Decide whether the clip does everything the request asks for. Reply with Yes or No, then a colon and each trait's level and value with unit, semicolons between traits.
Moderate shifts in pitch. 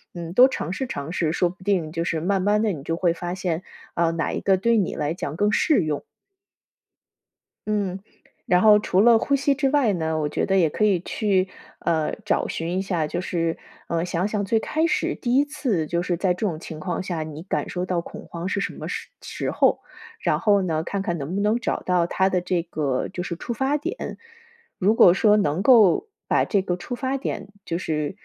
Yes: average, 4.0 semitones